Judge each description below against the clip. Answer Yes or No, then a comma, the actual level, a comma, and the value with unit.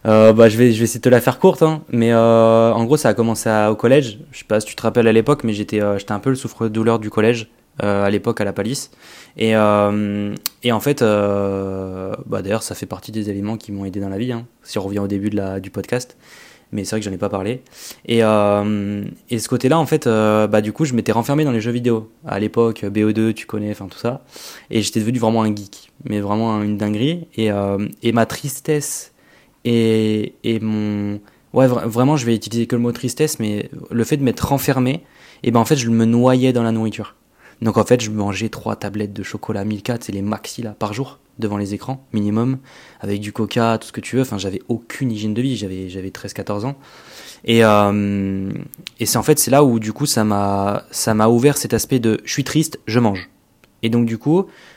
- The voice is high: No, low, 110 Hz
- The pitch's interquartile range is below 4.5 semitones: Yes, average, 2.7 semitones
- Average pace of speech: No, fast, 245 wpm